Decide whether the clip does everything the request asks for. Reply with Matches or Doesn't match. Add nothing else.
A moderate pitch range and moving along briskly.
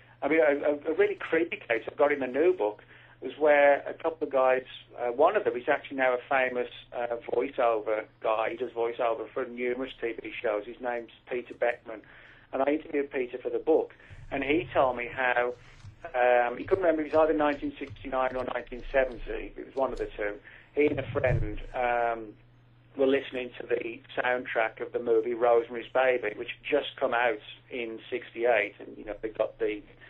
Doesn't match